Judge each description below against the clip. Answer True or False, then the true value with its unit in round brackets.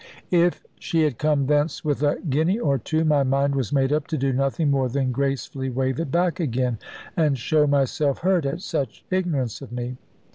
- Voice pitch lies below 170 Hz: True (140 Hz)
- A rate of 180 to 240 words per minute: True (195 wpm)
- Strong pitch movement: False (2.9 semitones)